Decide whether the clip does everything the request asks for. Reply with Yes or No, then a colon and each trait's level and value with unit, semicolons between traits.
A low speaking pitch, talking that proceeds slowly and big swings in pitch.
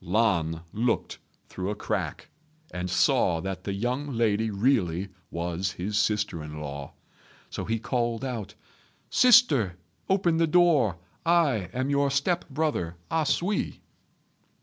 Yes: low, 115 Hz; slow, 130 wpm; wide, 7.5 semitones